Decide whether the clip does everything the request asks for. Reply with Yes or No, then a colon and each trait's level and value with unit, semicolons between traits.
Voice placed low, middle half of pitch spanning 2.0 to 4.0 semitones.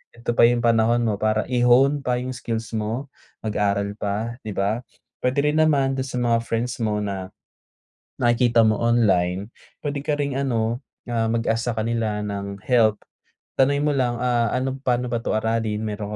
Yes: low, 115 Hz; narrow, 2.6 semitones